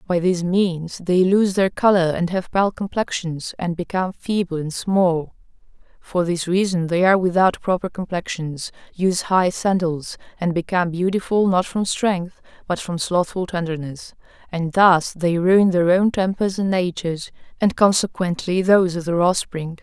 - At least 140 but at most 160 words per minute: Yes, average, 155 wpm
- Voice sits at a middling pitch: Yes, medium, 180 Hz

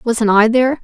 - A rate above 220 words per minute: No, fast, 215 wpm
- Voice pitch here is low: No, high, 235 Hz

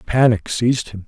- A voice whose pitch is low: Yes, low, 115 Hz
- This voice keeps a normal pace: Yes, average, 170 wpm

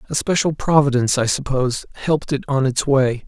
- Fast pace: No, average, 185 wpm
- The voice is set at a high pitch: No, low, 135 Hz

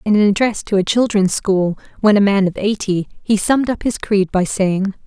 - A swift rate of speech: Yes, fast, 225 wpm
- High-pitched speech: Yes, high, 200 Hz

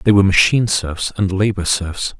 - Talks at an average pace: Yes, average, 190 wpm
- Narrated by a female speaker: No, male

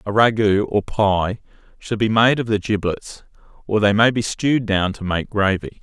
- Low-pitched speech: Yes, low, 105 Hz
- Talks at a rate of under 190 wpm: No, average, 195 wpm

